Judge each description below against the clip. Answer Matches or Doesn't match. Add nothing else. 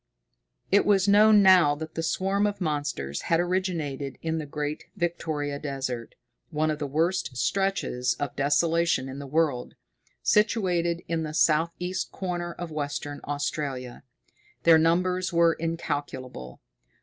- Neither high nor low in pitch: Matches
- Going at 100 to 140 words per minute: Matches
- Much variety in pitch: Doesn't match